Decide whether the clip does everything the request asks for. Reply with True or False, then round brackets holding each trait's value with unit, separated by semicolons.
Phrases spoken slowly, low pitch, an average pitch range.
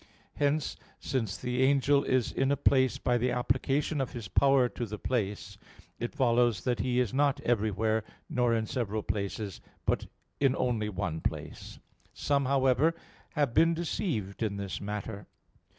False (155 wpm; 125 Hz; 4.2 semitones)